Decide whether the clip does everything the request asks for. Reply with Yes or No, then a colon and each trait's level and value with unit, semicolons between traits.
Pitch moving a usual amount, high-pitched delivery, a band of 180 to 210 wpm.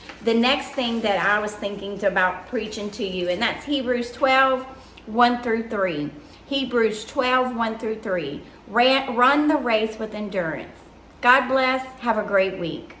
No: average, 4.2 semitones; high, 230 Hz; average, 155 wpm